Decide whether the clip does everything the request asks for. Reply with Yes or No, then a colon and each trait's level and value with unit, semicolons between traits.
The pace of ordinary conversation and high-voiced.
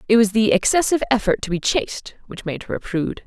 No: fast, 240 wpm; high, 215 Hz